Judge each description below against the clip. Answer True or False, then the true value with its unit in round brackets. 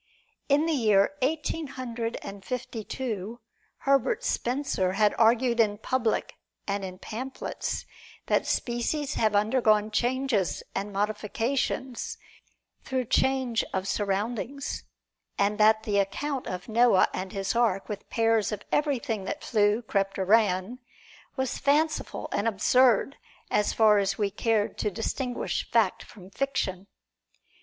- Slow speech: True (130 wpm)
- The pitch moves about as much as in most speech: True (4.1 semitones)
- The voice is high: True (225 Hz)